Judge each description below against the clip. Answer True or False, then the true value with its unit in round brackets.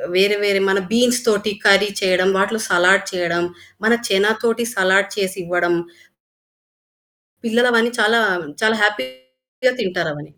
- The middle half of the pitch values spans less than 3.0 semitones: False (3.5 semitones)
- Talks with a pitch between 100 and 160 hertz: False (200 Hz)